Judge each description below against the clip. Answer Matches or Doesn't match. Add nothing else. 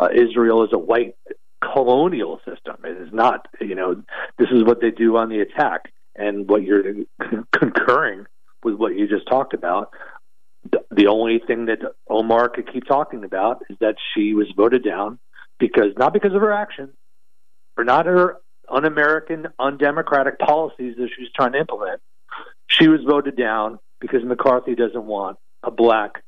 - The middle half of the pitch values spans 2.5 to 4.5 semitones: Doesn't match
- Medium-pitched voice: Doesn't match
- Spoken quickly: Doesn't match